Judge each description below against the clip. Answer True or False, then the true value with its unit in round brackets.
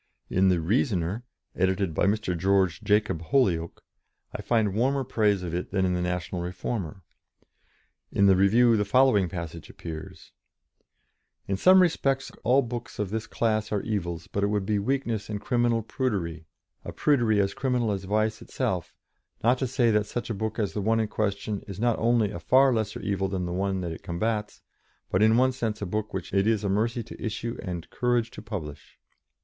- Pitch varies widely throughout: False (3.7 semitones)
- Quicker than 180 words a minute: True (190 wpm)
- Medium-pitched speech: False (105 Hz)